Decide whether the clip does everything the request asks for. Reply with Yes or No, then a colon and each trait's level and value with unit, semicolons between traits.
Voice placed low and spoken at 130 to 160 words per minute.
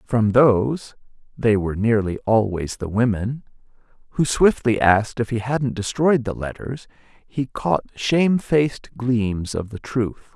Yes: low, 115 Hz; slow, 135 wpm